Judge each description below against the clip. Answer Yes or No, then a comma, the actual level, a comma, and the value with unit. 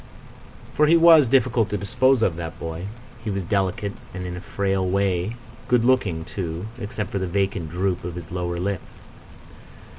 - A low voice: Yes, very low, 95 Hz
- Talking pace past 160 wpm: Yes, average, 175 wpm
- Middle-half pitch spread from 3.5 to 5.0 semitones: Yes, average, 4.1 semitones